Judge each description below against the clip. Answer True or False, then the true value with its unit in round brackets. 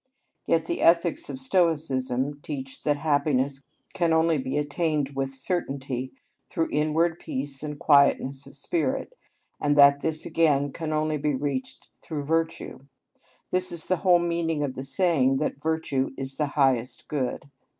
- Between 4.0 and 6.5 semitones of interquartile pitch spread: False (3.0 semitones)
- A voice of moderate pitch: True (145 Hz)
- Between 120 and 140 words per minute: False (155 wpm)